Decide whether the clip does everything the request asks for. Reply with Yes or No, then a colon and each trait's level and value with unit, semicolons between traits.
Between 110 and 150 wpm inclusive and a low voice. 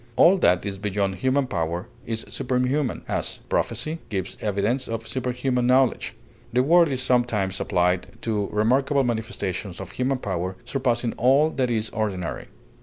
Yes: average, 145 wpm; low, 120 Hz